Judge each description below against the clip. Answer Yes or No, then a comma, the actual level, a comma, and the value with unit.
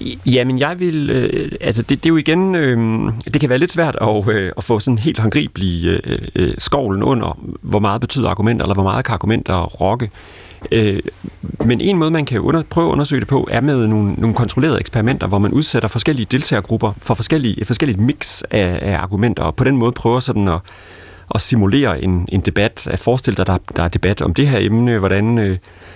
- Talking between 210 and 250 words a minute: Yes, average, 215 wpm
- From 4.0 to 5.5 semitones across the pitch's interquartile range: Yes, average, 4.6 semitones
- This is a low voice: Yes, low, 115 Hz